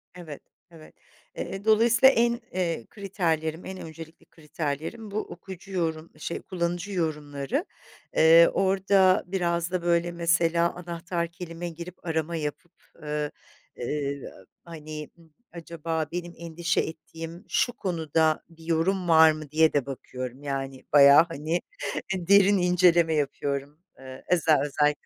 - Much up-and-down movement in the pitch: No, narrow, 2.5 semitones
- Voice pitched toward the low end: No, medium, 165 Hz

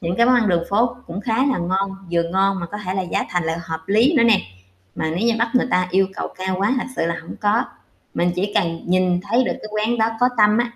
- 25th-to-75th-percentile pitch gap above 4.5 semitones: No, average, 4.2 semitones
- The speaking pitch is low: No, high, 195 Hz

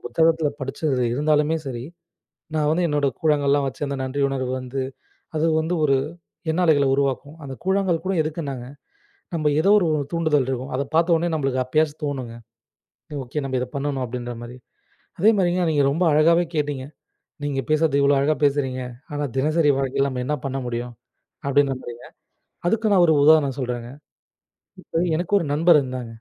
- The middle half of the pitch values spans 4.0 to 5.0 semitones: No, average, 3.2 semitones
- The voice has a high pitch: No, medium, 145 Hz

